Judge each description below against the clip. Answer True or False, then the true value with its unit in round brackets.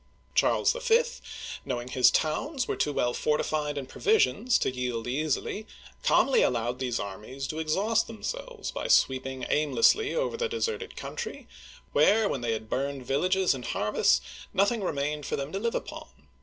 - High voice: False (150 Hz)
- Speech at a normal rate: True (160 wpm)